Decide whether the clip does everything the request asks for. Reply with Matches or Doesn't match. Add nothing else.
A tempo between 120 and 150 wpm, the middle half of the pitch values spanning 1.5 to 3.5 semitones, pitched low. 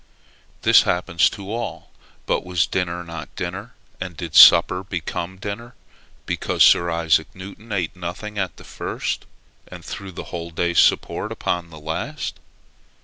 Matches